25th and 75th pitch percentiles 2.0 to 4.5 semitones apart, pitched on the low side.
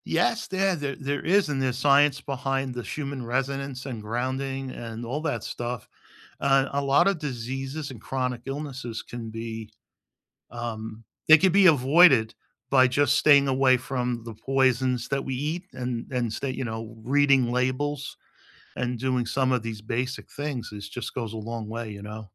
Yes: average, 2.9 semitones; low, 130 Hz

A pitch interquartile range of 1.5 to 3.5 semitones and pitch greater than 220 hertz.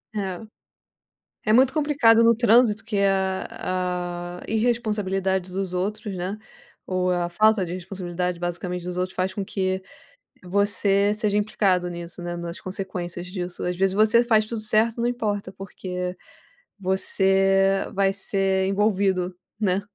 No: narrow, 2.6 semitones; high, 195 Hz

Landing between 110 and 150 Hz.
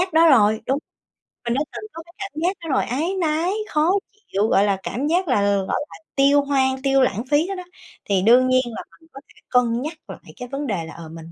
No: very high, 270 Hz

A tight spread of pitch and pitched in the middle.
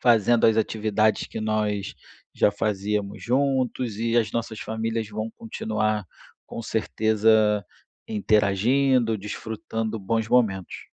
No: narrow, 1.4 semitones; low, 110 Hz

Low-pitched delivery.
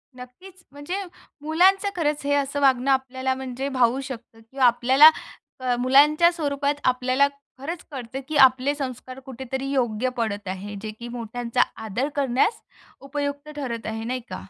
No: very high, 265 Hz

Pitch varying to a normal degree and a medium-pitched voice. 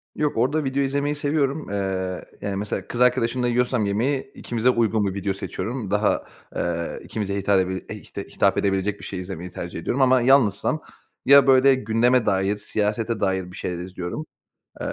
No: average, 5.0 semitones; low, 110 Hz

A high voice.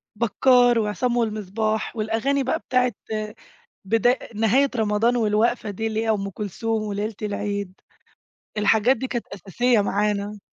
Yes: high, 220 Hz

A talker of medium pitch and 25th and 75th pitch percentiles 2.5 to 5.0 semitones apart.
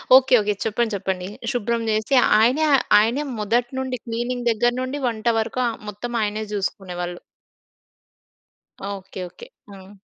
No: high, 225 Hz; average, 3.1 semitones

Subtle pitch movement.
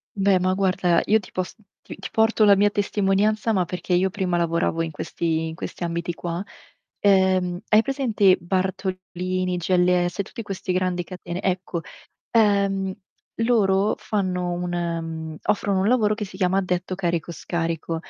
Yes: narrow, 2.2 semitones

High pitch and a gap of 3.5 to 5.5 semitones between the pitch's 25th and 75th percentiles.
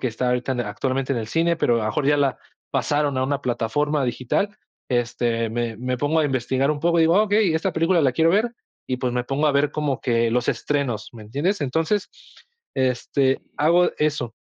No: low, 135 Hz; average, 3.9 semitones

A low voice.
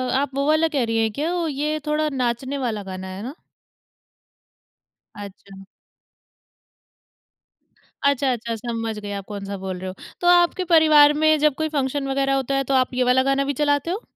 No: very high, 270 Hz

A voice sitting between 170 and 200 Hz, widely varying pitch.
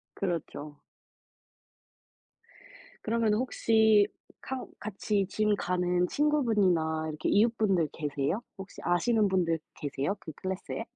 No: high, 190 Hz; average, 4.8 semitones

